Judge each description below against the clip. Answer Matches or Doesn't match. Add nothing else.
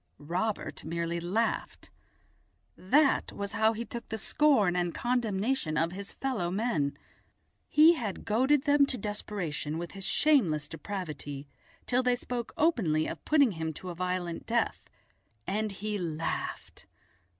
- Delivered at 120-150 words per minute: Matches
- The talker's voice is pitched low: Doesn't match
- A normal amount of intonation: Doesn't match